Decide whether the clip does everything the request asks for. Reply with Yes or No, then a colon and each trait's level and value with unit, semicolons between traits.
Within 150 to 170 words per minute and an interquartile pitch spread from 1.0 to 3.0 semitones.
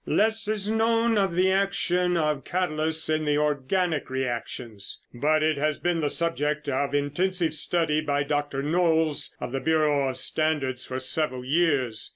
No: average, 160 wpm; average, 3.7 semitones